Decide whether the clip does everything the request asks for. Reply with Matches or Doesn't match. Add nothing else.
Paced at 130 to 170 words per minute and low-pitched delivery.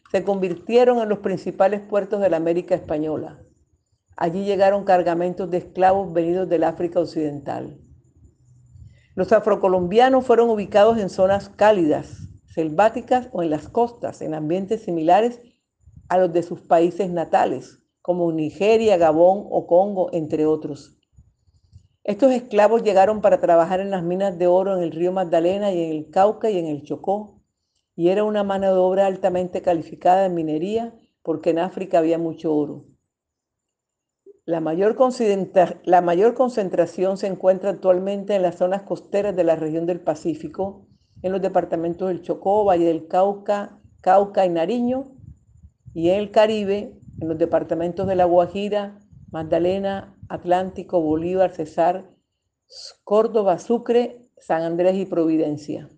Doesn't match